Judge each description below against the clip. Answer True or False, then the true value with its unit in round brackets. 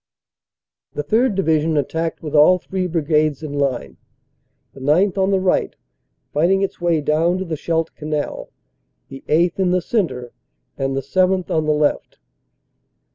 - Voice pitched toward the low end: False (160 Hz)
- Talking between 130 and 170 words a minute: True (155 wpm)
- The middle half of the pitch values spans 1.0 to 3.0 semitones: False (3.6 semitones)